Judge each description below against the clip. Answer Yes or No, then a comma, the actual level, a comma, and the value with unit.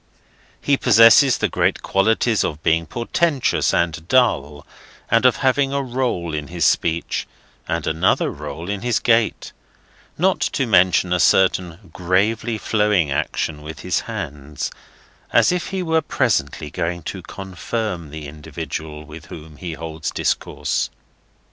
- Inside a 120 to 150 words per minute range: Yes, average, 140 wpm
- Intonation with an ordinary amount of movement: No, wide, 6.7 semitones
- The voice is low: Yes, very low, 90 Hz